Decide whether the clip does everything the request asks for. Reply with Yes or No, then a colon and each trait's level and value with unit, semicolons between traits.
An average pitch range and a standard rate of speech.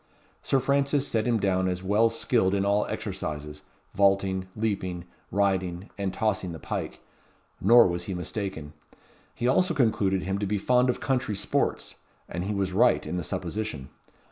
Yes: average, 3.2 semitones; average, 165 wpm